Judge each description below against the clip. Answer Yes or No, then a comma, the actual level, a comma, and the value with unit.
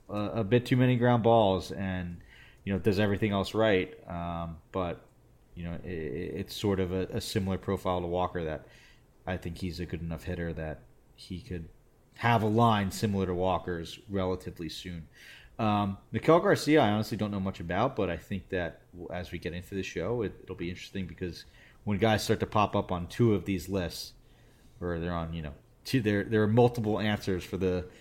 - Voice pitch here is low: Yes, very low, 95 Hz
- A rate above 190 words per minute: Yes, average, 200 wpm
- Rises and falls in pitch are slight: No, average, 3.7 semitones